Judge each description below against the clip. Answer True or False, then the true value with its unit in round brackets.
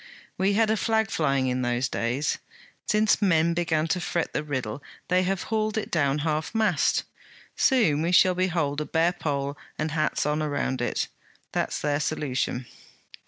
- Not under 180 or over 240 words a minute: False (170 wpm)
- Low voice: False (155 Hz)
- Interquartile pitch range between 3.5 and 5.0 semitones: True (4.6 semitones)